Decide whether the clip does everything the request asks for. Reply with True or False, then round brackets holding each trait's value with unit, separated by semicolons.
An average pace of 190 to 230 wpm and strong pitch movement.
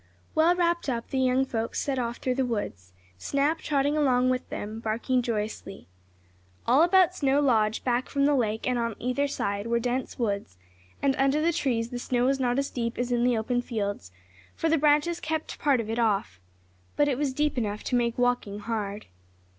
False (200 wpm; 3.6 semitones)